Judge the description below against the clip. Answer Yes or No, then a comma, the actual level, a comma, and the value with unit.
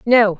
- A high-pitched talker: Yes, high, 220 Hz